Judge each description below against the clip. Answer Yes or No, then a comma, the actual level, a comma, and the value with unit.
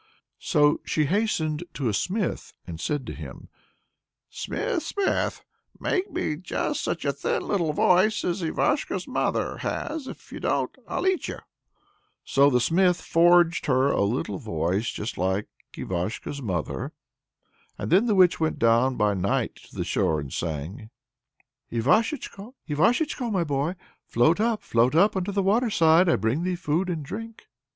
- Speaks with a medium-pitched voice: Yes, medium, 160 Hz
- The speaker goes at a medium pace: Yes, average, 155 wpm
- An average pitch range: No, wide, 8.7 semitones